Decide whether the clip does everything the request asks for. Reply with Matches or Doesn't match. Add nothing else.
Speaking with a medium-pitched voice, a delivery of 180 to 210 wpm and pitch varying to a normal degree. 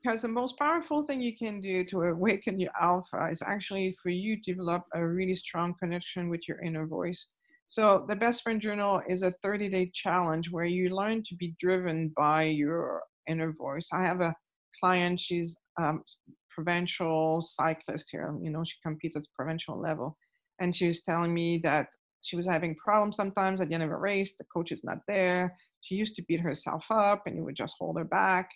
Matches